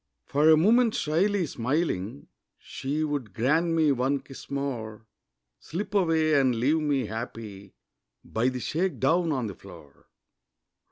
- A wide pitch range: Yes, wide, 5.8 semitones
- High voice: No, medium, 140 Hz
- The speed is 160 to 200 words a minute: No, slow, 135 wpm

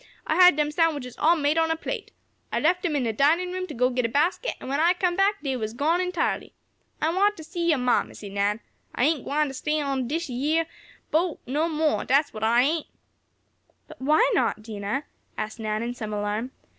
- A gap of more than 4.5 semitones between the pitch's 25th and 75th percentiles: Yes, average, 5.3 semitones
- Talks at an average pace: No, fast, 225 wpm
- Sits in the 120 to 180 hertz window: No, very high, 295 Hz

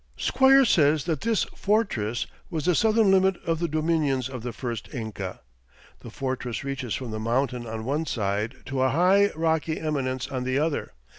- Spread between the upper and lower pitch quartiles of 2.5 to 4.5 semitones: No, average, 5.3 semitones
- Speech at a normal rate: Yes, average, 175 wpm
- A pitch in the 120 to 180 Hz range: Yes, medium, 140 Hz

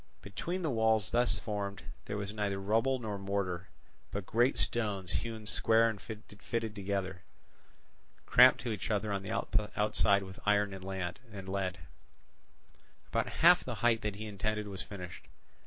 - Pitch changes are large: No, narrow, 2.4 semitones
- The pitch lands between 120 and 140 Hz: No, low, 105 Hz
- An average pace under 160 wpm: Yes, average, 150 wpm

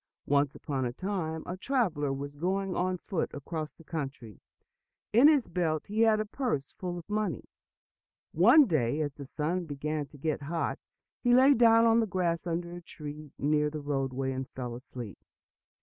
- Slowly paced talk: No, average, 180 wpm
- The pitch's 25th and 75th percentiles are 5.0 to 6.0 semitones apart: Yes, average, 5.3 semitones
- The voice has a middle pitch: Yes, medium, 160 Hz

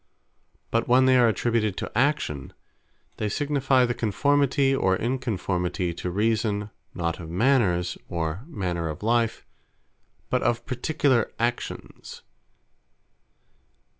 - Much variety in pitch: Yes, wide, 5.8 semitones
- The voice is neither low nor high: No, low, 115 Hz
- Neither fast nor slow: No, slow, 110 wpm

